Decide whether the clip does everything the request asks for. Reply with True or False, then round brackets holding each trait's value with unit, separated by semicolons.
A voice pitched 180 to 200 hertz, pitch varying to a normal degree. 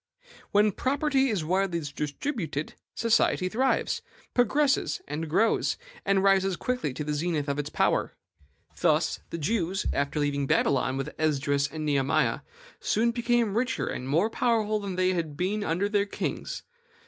False (185 Hz; 6.9 semitones)